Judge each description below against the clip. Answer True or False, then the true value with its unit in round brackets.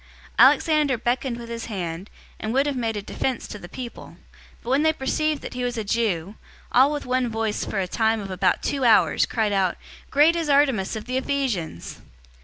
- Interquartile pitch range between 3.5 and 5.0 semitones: True (4.5 semitones)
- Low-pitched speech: False (235 Hz)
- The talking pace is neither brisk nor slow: False (210 wpm)